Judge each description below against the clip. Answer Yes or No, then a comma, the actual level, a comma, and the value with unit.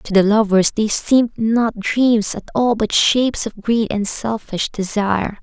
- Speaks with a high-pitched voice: Yes, high, 220 Hz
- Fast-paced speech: No, average, 175 wpm